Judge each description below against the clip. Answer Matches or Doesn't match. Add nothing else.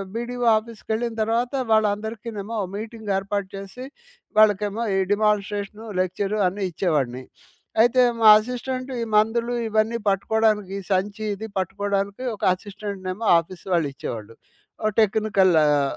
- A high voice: Matches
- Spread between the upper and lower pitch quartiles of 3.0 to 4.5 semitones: Doesn't match